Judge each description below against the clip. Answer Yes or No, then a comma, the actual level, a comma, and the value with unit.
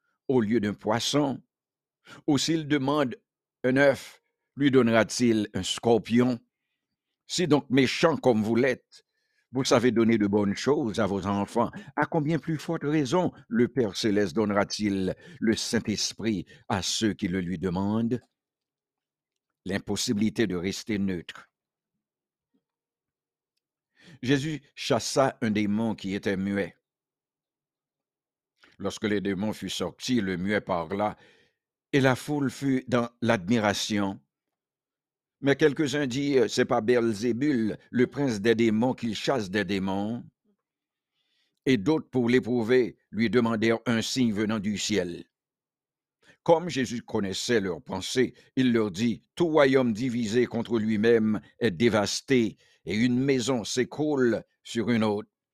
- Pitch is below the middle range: Yes, low, 115 Hz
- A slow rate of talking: Yes, slow, 125 wpm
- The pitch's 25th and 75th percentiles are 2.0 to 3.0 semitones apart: No, average, 4.2 semitones